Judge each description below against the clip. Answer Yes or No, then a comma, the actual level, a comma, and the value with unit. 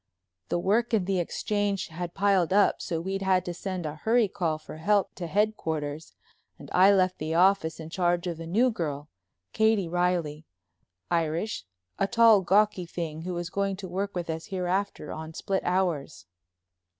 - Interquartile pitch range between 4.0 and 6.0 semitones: No, average, 3.3 semitones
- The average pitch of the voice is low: No, medium, 180 Hz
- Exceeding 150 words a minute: Yes, average, 175 wpm